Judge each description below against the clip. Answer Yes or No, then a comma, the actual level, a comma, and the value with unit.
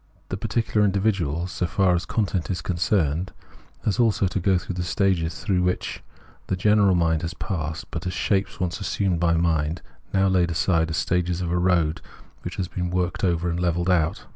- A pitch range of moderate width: No, narrow, 2.3 semitones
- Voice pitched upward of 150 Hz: No, very low, 90 Hz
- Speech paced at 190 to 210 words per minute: Yes, average, 195 wpm